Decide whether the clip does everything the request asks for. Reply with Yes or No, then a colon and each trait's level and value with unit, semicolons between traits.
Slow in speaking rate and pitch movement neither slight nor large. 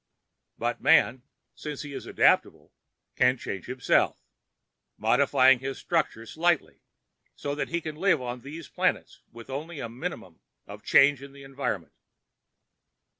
Yes: slow, 125 wpm; average, 3.3 semitones